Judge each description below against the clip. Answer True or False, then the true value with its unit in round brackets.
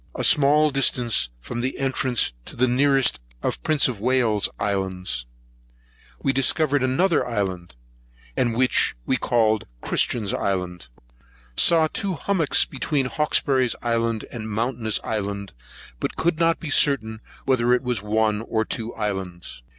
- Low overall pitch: True (120 Hz)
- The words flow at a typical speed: False (130 wpm)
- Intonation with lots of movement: False (4.5 semitones)